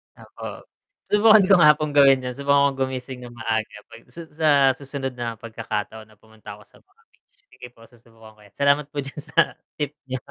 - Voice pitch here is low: Yes, low, 130 Hz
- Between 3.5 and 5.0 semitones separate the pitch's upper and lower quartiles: Yes, average, 4.3 semitones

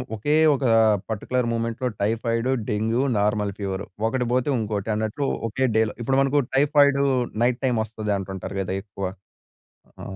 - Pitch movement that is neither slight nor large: Yes, average, 3.6 semitones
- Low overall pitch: Yes, low, 115 Hz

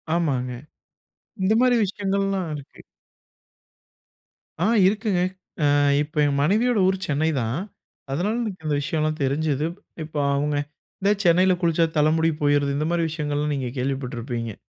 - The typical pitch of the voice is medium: Yes, medium, 155 Hz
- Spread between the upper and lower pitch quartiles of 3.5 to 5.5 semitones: Yes, average, 4.7 semitones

